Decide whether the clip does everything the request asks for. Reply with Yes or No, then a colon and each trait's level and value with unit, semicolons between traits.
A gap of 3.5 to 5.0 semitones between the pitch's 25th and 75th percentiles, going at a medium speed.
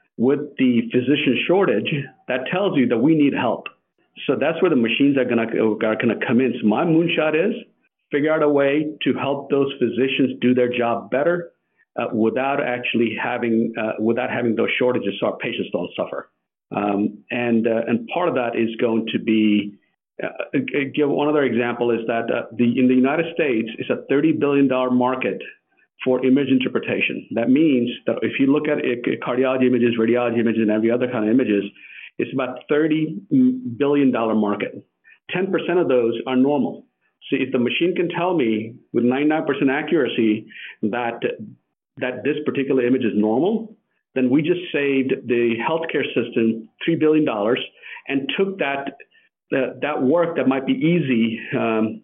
Yes: average, 3.9 semitones; average, 170 wpm